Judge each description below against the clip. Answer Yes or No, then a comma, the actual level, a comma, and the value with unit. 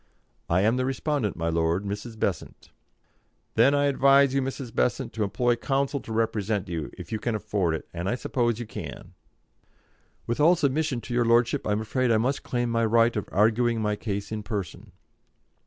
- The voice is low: Yes, low, 115 Hz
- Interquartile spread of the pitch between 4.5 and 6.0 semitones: No, average, 3.7 semitones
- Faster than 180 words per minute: Yes, average, 190 wpm